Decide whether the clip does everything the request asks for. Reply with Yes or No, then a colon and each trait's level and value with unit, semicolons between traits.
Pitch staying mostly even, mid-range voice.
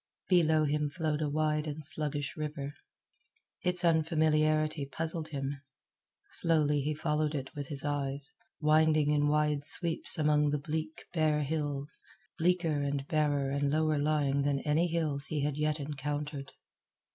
Yes: narrow, 1.5 semitones; medium, 150 Hz